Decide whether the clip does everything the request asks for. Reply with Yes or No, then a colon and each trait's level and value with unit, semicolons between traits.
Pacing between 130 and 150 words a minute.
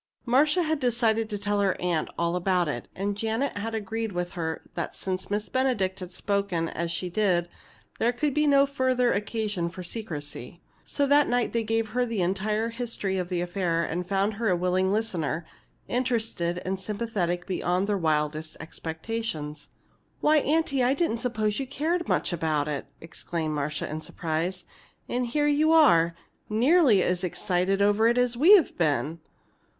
No: average, 170 wpm